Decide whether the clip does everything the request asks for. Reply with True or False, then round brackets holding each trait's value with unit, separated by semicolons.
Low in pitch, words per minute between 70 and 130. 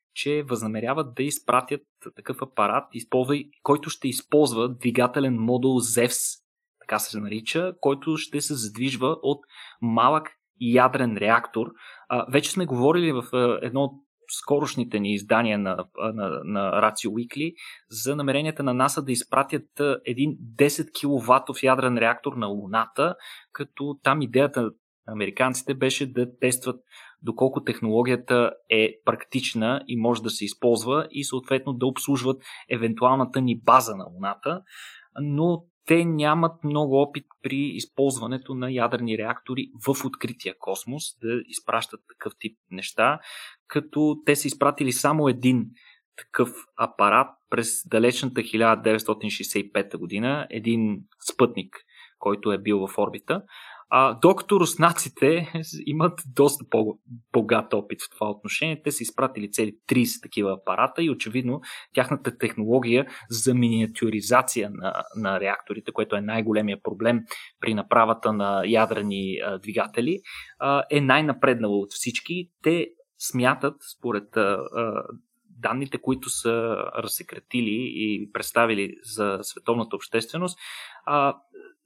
True (130 Hz; 120 wpm)